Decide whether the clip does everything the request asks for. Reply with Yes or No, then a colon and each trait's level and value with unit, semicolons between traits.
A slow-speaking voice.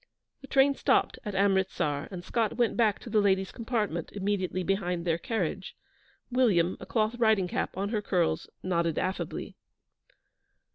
No: average, 150 wpm